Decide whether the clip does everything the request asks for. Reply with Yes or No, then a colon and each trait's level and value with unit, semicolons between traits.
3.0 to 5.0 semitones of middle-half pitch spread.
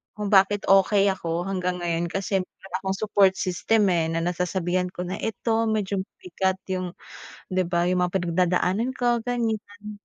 No: narrow, 2.6 semitones